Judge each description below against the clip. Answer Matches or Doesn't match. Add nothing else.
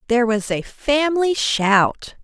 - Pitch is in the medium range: Doesn't match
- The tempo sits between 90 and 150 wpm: Matches